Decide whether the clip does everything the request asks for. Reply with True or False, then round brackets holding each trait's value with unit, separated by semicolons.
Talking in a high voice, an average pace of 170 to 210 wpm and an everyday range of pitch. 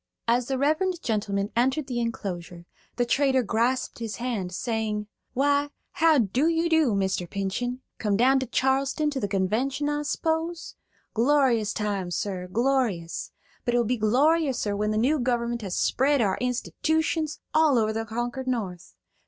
False (245 Hz; 160 wpm; 4.8 semitones)